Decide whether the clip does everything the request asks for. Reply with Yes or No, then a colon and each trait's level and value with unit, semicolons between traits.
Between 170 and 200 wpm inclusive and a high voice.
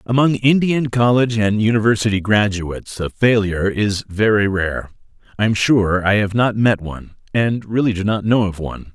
No: average, 175 wpm; low, 105 Hz